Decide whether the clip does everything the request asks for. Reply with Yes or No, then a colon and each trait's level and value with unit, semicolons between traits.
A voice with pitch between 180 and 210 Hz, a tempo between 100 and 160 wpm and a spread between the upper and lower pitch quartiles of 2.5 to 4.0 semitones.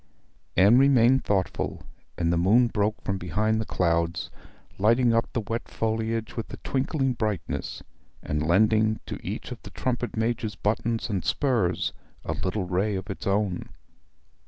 No: low, 110 Hz; average, 155 wpm; average, 3.6 semitones